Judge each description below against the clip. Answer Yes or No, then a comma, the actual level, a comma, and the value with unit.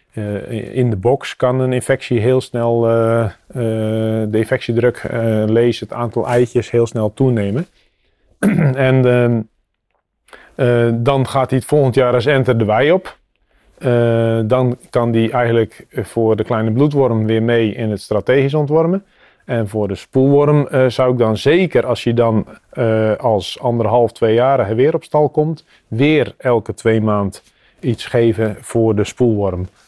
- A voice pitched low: Yes, low, 120 Hz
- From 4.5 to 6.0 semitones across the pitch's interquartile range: No, narrow, 2.6 semitones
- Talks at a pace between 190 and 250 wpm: No, average, 160 wpm